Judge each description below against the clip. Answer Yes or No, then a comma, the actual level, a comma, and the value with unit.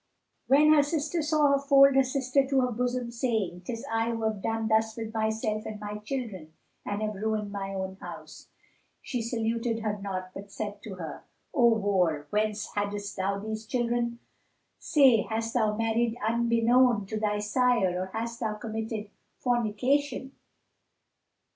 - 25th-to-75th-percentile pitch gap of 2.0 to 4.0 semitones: Yes, average, 2.9 semitones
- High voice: Yes, high, 225 Hz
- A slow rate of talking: No, average, 160 wpm